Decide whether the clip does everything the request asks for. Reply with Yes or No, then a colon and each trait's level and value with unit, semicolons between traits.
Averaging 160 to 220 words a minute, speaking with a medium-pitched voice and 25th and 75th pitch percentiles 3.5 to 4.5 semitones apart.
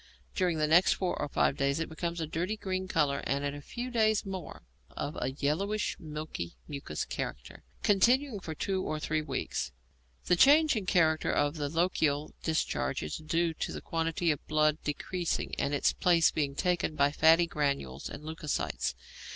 Yes: average, 180 wpm; medium, 160 Hz; average, 3.9 semitones